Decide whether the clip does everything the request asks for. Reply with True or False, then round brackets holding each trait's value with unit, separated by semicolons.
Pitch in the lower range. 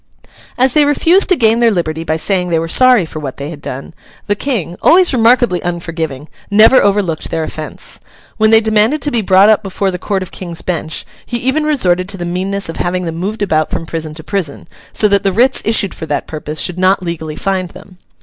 False (185 Hz)